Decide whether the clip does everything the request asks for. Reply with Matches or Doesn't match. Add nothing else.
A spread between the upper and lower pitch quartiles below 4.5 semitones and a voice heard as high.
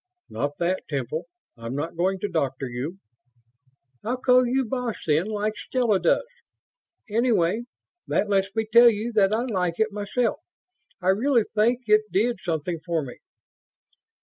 Doesn't match